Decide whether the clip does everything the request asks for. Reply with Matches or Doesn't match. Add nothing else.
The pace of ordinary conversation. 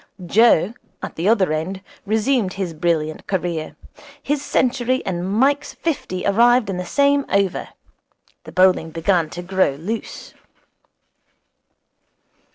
Doesn't match